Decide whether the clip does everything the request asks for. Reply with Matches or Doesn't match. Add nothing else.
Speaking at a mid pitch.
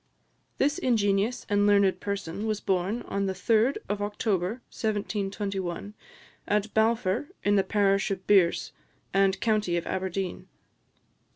Doesn't match